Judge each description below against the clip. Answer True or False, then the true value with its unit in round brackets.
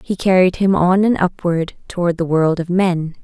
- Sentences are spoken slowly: False (205 wpm)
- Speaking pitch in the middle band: True (180 Hz)